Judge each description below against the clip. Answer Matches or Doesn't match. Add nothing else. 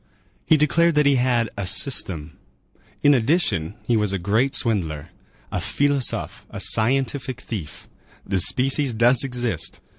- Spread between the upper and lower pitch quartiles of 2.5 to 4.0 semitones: Doesn't match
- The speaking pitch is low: Matches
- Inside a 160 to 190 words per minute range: Doesn't match